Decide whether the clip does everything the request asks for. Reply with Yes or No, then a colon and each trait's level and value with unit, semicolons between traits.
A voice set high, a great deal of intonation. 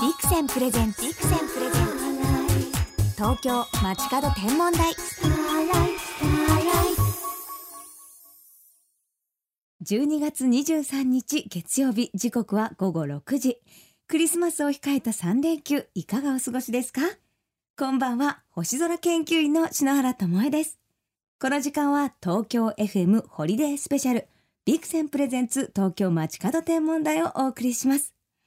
Yes: very high, 270 Hz; wide, 5.8 semitones